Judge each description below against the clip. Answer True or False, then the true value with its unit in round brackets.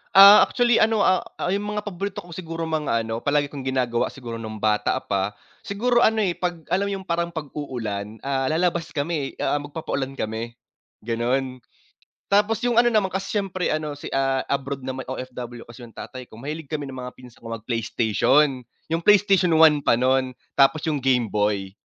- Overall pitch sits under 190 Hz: True (140 Hz)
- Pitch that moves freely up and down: True (6.4 semitones)